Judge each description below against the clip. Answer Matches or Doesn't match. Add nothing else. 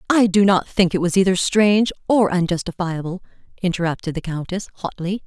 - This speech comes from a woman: Matches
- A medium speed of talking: Matches